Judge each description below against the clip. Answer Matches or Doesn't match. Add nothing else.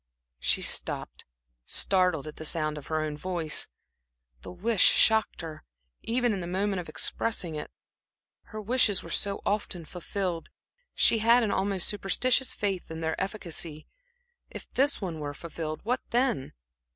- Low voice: Doesn't match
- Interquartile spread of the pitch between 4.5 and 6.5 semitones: Matches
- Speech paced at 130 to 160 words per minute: Matches